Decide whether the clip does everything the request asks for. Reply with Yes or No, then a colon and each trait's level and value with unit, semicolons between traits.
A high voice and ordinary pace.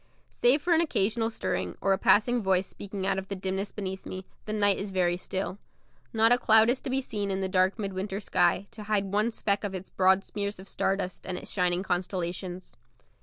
No: high, 195 Hz; fast, 220 wpm